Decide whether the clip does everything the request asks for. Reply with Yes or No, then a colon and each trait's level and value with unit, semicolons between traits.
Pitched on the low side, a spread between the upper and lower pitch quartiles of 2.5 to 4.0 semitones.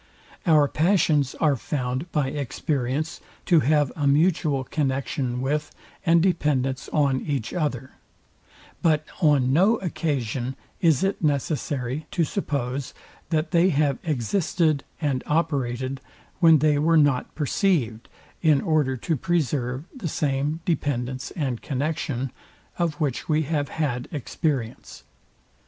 No: medium, 145 Hz; average, 3.3 semitones